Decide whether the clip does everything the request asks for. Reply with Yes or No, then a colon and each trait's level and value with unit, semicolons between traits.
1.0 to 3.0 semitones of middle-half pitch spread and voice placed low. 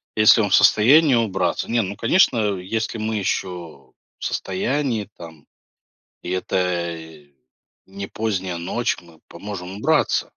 No: average, 3.9 semitones; low, 100 Hz